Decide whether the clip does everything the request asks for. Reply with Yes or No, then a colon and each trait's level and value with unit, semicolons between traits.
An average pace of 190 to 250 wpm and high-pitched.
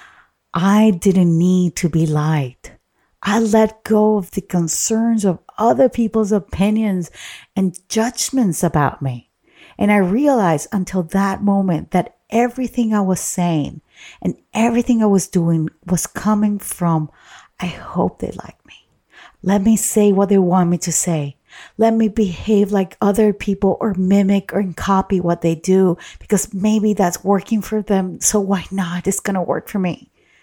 No: average, 160 wpm; high, 195 Hz